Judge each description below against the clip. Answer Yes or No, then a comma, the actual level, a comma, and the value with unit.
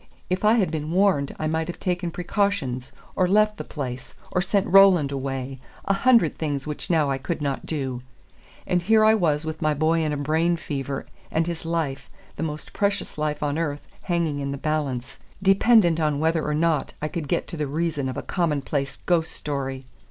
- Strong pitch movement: No, average, 3.6 semitones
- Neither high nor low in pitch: Yes, medium, 155 Hz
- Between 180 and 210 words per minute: Yes, average, 200 wpm